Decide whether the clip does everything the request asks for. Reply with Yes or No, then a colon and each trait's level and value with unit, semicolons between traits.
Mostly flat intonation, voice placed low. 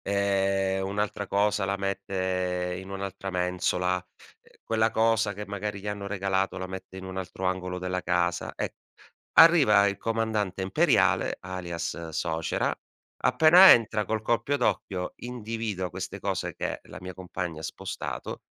Yes: narrow, 2.2 semitones; very low, 95 Hz